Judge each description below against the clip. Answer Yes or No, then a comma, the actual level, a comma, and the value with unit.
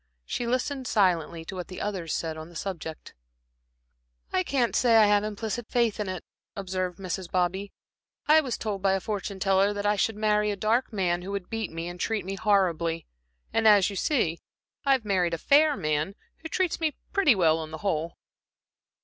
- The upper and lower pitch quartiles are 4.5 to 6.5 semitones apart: No, average, 4.0 semitones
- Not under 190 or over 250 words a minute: Yes, average, 195 wpm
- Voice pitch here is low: No, high, 195 Hz